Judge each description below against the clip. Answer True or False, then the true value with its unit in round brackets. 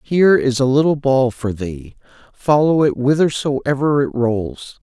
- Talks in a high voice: False (140 Hz)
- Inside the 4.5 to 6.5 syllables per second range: False (4.2 syllables/s)